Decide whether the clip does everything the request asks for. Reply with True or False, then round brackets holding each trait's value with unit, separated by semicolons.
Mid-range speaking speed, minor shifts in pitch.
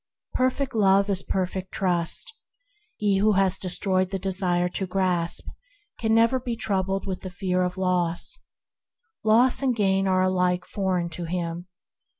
True (150 wpm; 2.1 semitones)